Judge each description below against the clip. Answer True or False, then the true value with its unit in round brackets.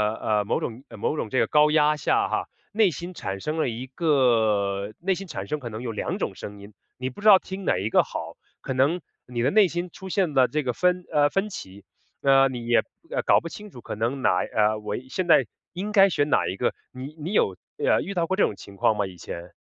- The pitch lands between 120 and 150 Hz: True (135 Hz)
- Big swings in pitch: True (8.2 semitones)